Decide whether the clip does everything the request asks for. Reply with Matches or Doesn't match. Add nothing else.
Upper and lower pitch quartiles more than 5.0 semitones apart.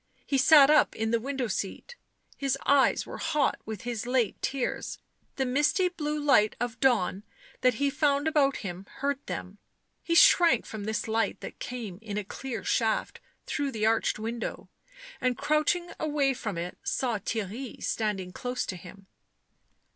Doesn't match